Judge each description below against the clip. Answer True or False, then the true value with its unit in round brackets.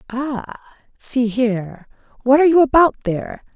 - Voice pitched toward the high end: True (255 Hz)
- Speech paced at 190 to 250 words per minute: False (135 wpm)